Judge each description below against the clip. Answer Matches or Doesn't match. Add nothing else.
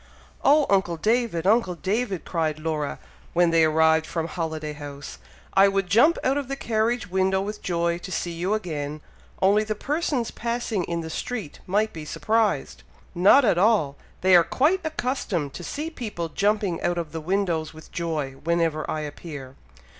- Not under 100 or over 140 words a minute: Doesn't match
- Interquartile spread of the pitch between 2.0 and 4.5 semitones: Doesn't match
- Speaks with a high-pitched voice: Doesn't match